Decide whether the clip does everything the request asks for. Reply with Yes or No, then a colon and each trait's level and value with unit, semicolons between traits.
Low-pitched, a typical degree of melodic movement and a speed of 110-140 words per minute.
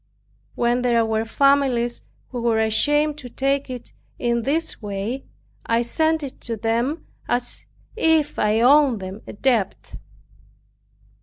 No: high, 245 Hz; average, 3.7 semitones; slow, 135 wpm